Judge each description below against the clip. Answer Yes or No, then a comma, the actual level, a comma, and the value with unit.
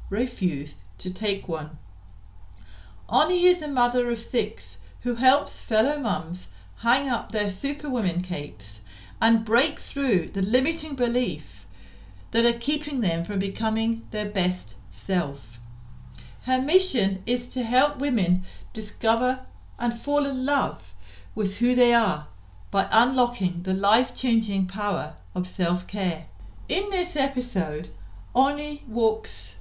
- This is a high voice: Yes, high, 210 Hz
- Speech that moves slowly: Yes, slow, 130 wpm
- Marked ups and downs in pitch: Yes, wide, 9.0 semitones